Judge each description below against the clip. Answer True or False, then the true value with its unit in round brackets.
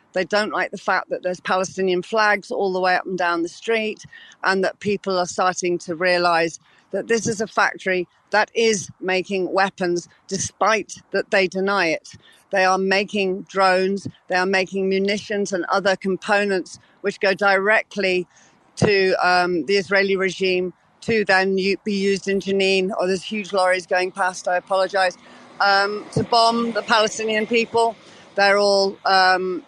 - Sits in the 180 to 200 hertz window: True (190 Hz)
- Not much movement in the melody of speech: True (1.6 semitones)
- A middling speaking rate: True (160 wpm)